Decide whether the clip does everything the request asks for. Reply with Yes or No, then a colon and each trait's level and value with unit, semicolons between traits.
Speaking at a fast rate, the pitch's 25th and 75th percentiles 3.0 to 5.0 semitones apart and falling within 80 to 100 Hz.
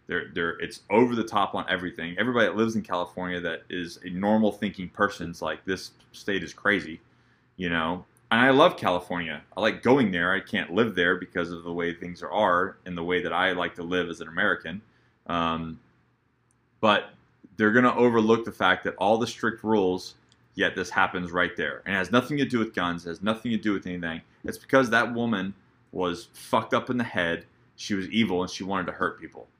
Yes: fast, 220 wpm; average, 4.4 semitones; very low, 95 Hz